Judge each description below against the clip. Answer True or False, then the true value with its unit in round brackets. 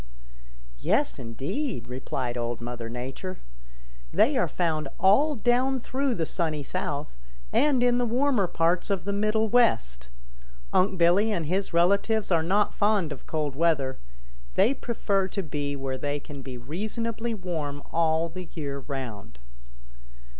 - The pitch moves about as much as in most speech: False (7.3 semitones)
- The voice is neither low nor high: True (170 Hz)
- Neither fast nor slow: True (145 wpm)